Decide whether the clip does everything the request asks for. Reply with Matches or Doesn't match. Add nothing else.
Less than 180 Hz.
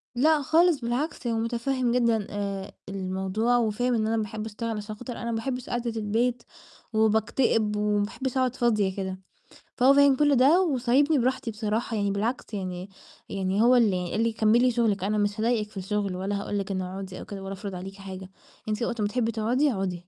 Doesn't match